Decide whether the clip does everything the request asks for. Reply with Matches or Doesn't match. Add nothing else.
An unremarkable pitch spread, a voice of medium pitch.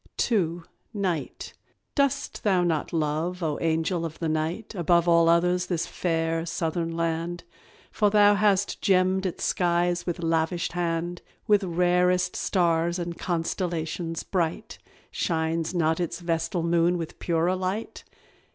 Doesn't match